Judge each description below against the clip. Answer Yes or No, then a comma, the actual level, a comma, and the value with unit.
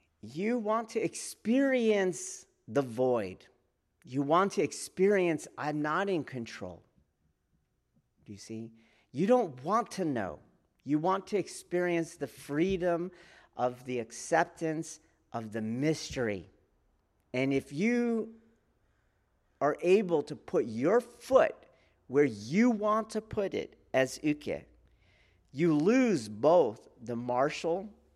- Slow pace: Yes, slow, 120 wpm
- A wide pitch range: Yes, wide, 8.1 semitones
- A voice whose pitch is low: No, medium, 165 Hz